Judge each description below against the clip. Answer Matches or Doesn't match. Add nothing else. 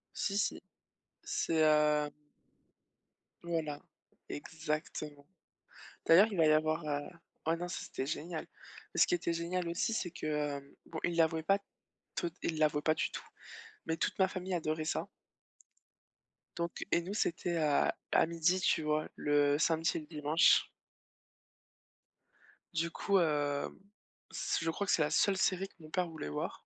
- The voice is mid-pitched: Matches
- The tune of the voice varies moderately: Doesn't match